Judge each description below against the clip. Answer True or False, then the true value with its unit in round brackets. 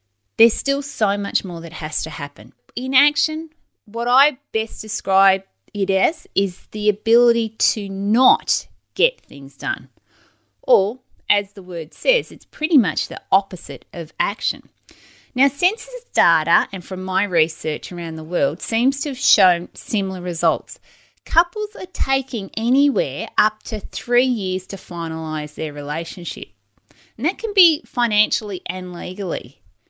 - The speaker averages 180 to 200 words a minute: False (145 wpm)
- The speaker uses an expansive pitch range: True (6.8 semitones)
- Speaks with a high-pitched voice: True (210 Hz)